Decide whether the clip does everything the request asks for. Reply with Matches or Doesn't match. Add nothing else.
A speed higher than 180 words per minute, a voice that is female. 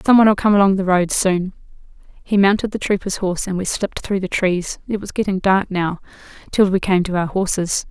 Matches